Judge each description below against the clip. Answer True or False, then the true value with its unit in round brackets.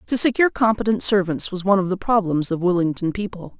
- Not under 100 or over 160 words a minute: False (200 wpm)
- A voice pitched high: True (195 Hz)